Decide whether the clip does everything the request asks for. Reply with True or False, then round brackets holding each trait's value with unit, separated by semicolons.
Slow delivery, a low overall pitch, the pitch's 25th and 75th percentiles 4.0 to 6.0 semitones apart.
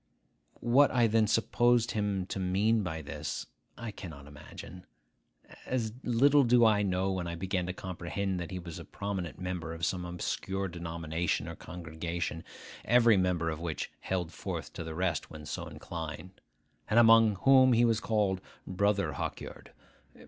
False (160 wpm; 95 Hz; 4.5 semitones)